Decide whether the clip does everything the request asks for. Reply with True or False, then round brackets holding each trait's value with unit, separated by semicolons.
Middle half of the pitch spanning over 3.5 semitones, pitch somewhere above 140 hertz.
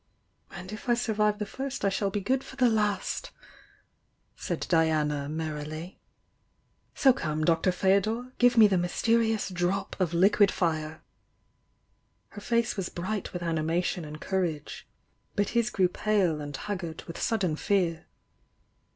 True (4.7 semitones; 190 Hz)